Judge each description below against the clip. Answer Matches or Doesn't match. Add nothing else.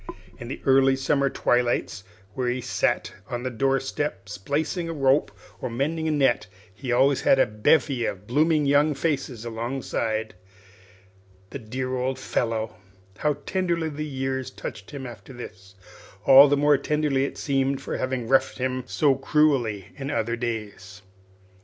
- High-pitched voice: Doesn't match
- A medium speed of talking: Matches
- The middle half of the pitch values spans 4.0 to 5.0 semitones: Doesn't match